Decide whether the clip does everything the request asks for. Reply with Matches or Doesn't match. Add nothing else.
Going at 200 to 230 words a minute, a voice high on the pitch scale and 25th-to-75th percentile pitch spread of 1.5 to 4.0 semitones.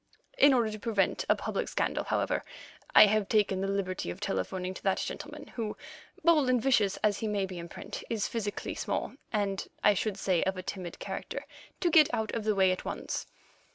Matches